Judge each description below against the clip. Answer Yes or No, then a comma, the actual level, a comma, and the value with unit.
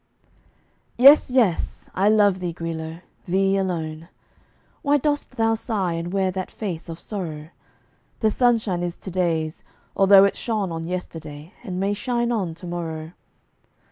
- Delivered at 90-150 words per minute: Yes, average, 145 wpm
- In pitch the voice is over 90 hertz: Yes, medium, 185 Hz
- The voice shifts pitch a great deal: No, average, 4.4 semitones